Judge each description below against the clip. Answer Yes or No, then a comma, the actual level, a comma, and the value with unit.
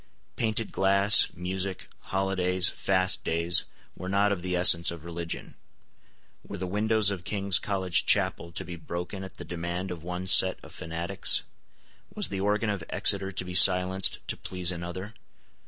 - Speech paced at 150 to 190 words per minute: Yes, average, 160 wpm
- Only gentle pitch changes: Yes, narrow, 2.0 semitones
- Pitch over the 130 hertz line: No, very low, 95 Hz